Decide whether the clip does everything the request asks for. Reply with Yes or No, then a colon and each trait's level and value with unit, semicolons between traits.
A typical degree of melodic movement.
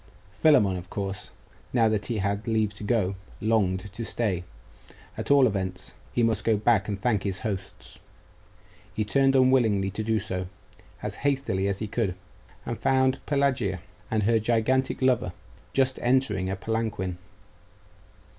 Yes: average, 3.9 semitones